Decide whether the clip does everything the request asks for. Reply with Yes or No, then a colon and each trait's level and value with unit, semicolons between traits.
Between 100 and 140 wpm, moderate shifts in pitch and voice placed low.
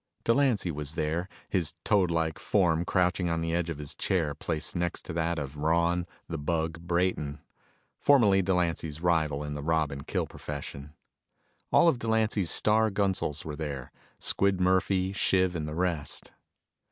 No: average, 155 wpm; average, 3.3 semitones; very low, 85 Hz